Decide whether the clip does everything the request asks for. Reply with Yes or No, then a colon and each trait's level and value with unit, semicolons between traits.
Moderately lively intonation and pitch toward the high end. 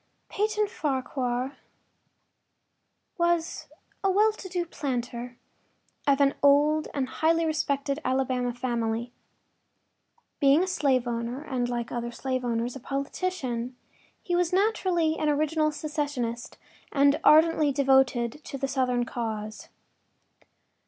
Yes: average, 4.2 semitones; very high, 275 Hz